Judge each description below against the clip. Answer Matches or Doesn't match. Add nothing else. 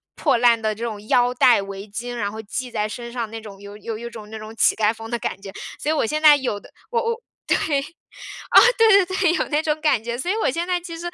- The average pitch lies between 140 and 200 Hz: Doesn't match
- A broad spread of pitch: Matches